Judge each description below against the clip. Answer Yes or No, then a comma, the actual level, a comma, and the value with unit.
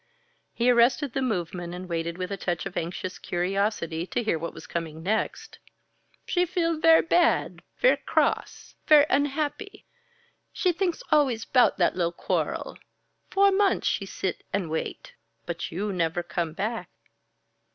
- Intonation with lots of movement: Yes, wide, 9.0 semitones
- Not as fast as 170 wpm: Yes, average, 150 wpm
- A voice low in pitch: No, high, 200 Hz